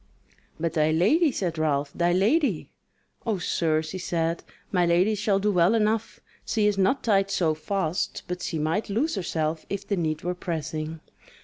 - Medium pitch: Yes, medium, 180 Hz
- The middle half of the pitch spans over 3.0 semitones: Yes, average, 4.2 semitones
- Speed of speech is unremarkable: Yes, average, 175 wpm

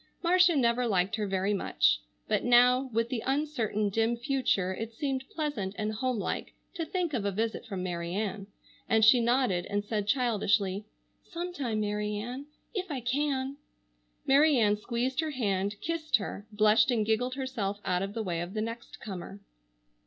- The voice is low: No, high, 225 Hz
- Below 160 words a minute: No, average, 175 wpm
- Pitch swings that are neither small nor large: Yes, average, 4.4 semitones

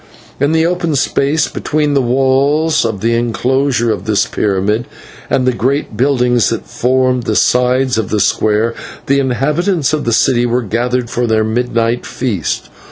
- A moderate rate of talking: Yes, average, 165 wpm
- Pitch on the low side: Yes, low, 125 Hz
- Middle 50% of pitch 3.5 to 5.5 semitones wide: No, average, 3.1 semitones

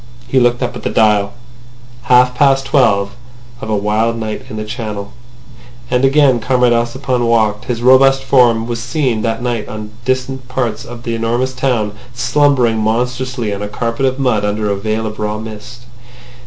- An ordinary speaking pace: Yes, average, 175 wpm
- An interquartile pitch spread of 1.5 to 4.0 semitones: Yes, average, 2.9 semitones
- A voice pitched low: Yes, low, 120 Hz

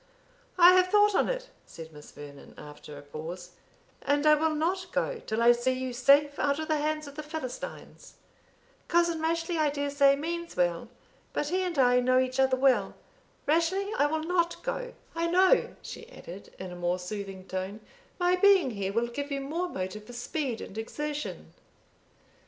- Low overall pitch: No, very high, 285 Hz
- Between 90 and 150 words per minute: No, average, 185 wpm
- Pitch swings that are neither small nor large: No, wide, 7.3 semitones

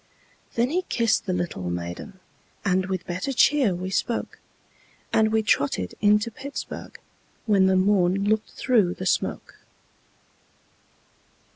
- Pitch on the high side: Yes, high, 195 Hz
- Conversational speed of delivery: No, slow, 125 wpm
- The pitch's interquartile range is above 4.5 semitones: No, average, 3.4 semitones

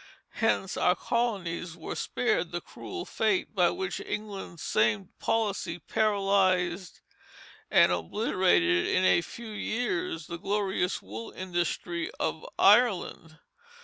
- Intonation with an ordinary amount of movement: Yes, average, 3.8 semitones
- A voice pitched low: No, medium, 185 Hz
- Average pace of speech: No, slow, 115 wpm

